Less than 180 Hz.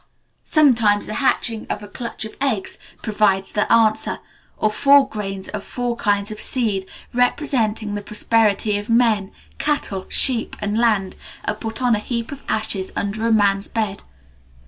No: high, 215 Hz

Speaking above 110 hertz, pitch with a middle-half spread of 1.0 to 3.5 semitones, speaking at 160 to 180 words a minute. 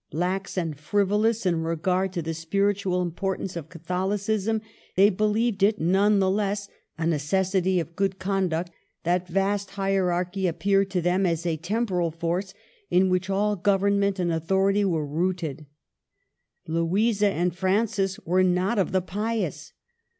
No: high, 190 Hz; narrow, 2.4 semitones; average, 145 wpm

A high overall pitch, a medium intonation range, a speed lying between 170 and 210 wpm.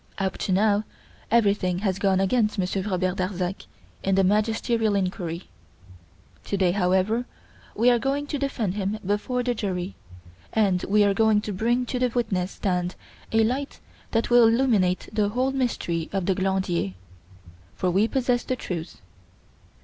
No: high, 205 Hz; average, 3.8 semitones; average, 155 wpm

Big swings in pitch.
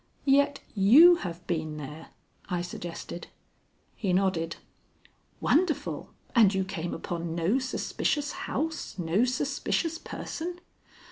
Yes: wide, 9.0 semitones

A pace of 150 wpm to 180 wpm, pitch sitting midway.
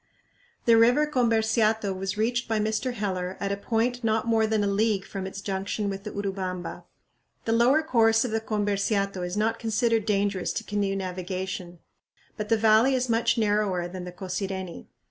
No: average, 175 wpm; high, 210 Hz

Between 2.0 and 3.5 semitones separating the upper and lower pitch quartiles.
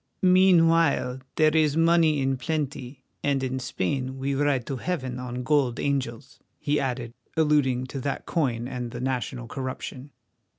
Yes: average, 3.0 semitones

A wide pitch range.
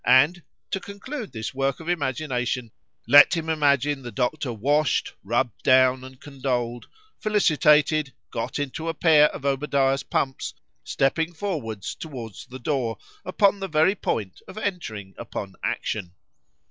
No: average, 4.5 semitones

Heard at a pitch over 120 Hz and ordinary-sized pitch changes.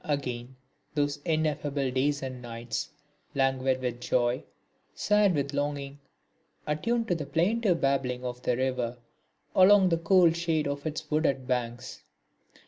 Yes: medium, 140 Hz; average, 4.0 semitones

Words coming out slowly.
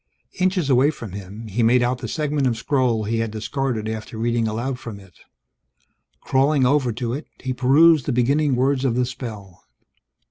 No: average, 180 wpm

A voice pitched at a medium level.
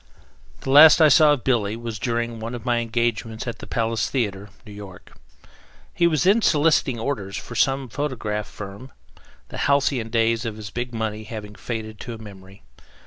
No: low, 115 Hz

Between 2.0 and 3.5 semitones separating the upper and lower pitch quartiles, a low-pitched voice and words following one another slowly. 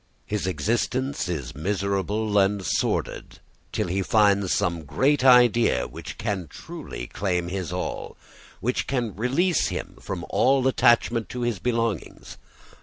No: average, 4.8 semitones; low, 105 Hz; slow, 130 wpm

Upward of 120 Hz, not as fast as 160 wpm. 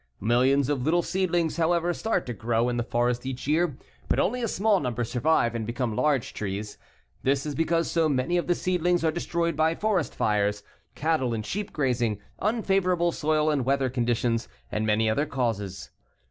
No: medium, 140 Hz; average, 180 wpm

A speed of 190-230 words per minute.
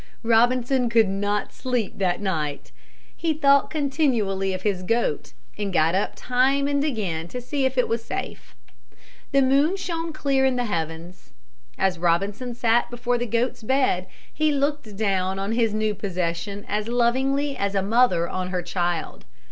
No: average, 165 wpm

